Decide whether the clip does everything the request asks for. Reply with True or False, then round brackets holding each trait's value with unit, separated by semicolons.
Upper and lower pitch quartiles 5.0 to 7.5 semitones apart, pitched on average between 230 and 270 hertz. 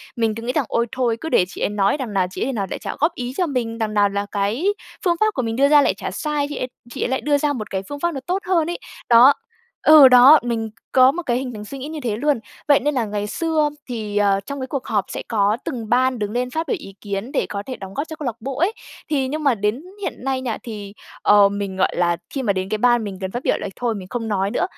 True (5.4 semitones; 245 Hz)